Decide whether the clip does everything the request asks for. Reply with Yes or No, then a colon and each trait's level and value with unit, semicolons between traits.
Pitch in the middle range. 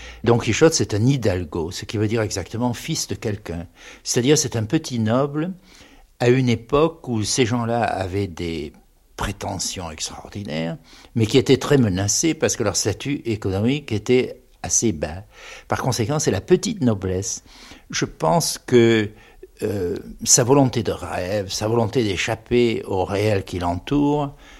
No: low, 115 Hz